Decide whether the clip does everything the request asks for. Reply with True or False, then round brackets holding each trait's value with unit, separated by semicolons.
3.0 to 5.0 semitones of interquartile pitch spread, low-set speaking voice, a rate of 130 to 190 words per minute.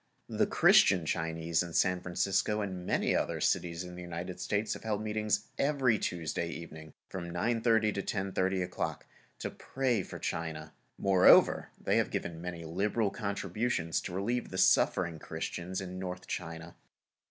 True (3.7 semitones; 90 Hz; 155 wpm)